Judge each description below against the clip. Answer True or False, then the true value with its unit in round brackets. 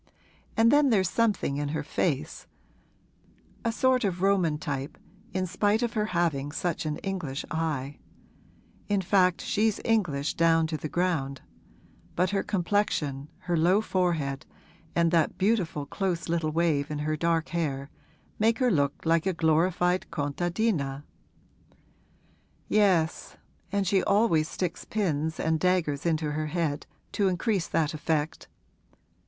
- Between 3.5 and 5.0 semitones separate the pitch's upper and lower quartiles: True (4.1 semitones)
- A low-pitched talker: False (170 Hz)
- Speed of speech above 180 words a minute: False (135 wpm)